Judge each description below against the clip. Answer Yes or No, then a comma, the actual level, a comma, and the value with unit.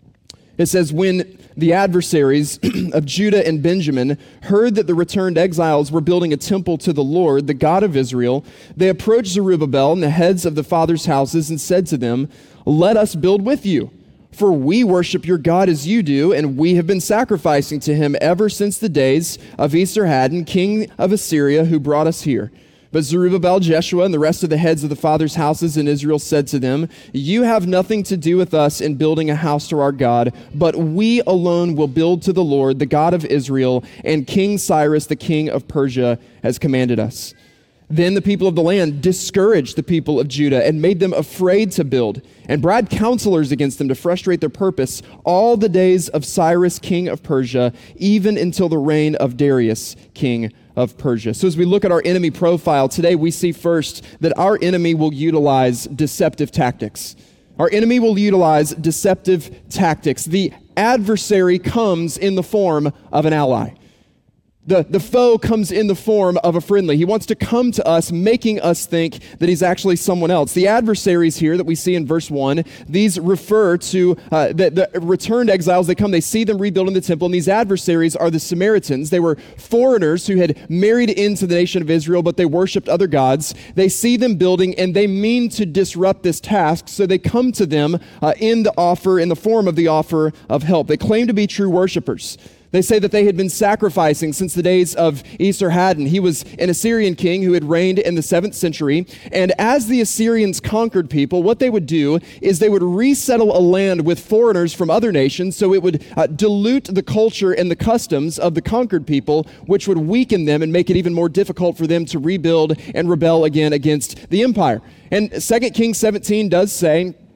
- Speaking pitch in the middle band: Yes, medium, 175 Hz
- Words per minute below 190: No, average, 200 wpm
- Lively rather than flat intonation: No, average, 4.1 semitones